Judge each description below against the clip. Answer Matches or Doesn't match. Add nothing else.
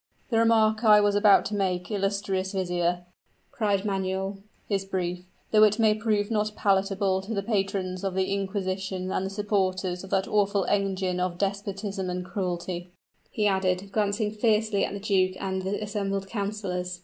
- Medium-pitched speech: Doesn't match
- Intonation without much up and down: Matches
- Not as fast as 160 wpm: Doesn't match